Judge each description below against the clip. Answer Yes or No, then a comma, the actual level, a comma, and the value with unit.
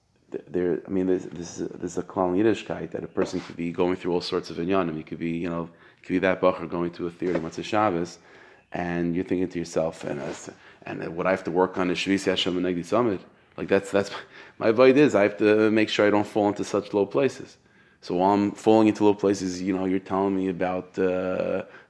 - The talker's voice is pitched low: Yes, very low, 95 Hz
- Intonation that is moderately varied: No, narrow, 2.1 semitones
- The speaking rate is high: Yes, fast, 250 wpm